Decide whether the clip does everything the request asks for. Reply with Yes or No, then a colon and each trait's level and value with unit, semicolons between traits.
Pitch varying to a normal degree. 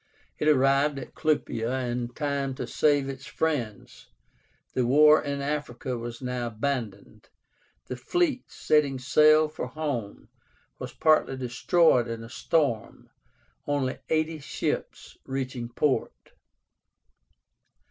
Yes: average, 3.6 semitones